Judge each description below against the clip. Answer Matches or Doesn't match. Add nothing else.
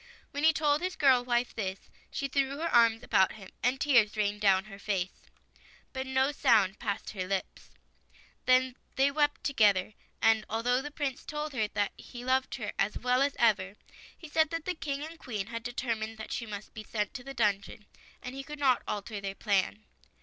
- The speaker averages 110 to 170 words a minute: Doesn't match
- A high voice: Matches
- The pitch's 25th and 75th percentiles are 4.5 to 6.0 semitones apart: Matches